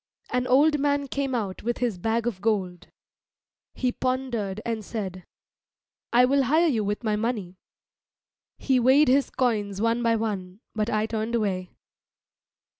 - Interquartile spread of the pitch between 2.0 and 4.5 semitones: Yes, average, 3.6 semitones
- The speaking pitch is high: Yes, high, 230 Hz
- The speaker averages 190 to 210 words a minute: No, average, 150 wpm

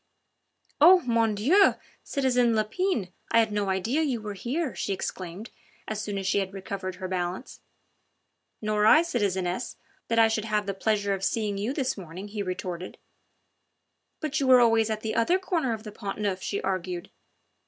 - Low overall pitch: No, high, 215 Hz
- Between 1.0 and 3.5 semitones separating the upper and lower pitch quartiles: No, average, 3.9 semitones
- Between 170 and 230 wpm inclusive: Yes, average, 175 wpm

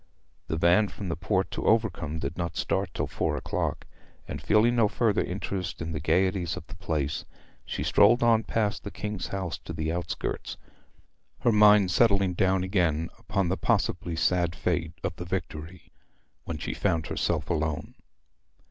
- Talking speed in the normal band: Yes, average, 165 wpm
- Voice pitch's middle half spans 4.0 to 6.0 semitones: No, average, 3.5 semitones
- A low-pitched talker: Yes, very low, 90 Hz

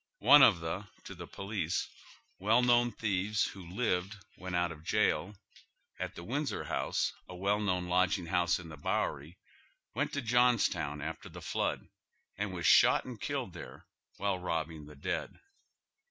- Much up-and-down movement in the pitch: No, average, 3.8 semitones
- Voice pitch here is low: Yes, very low, 95 Hz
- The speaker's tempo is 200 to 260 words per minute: No, average, 160 wpm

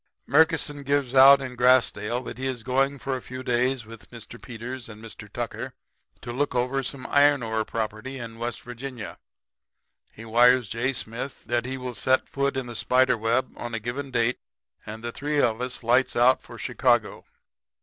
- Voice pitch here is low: Yes, low, 125 Hz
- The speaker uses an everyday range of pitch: No, narrow, 2.2 semitones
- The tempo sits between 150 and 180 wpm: No, average, 190 wpm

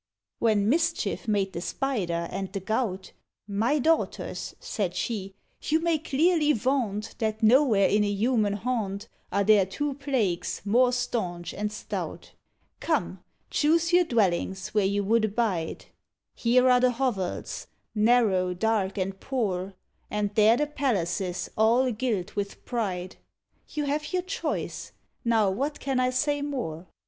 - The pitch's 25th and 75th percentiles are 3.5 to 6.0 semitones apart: Yes, average, 5.0 semitones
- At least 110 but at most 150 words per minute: Yes, average, 140 wpm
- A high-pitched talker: Yes, high, 220 Hz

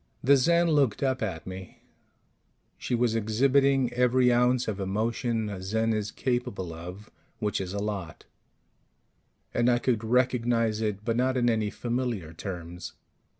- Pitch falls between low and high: No, low, 115 Hz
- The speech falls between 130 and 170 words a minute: Yes, average, 150 wpm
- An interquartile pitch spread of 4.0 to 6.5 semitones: No, average, 3.5 semitones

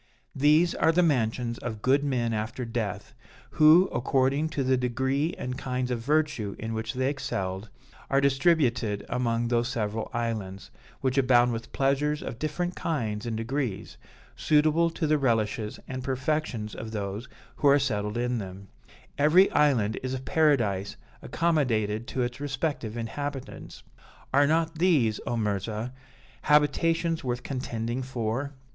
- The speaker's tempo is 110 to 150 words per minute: Yes, average, 145 wpm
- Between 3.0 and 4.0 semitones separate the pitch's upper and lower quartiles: No, average, 4.4 semitones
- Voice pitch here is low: Yes, low, 125 Hz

